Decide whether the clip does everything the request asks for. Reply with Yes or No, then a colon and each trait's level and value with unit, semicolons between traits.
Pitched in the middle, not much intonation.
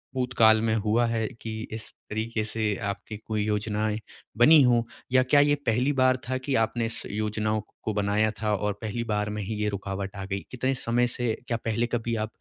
No: low, 110 Hz; narrow, 2.2 semitones